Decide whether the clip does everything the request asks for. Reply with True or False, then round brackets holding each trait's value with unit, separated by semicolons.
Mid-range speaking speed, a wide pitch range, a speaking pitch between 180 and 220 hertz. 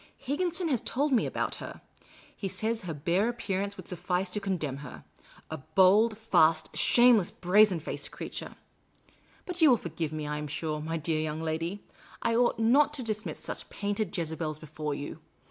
True (180 wpm; 6.1 semitones; 190 Hz)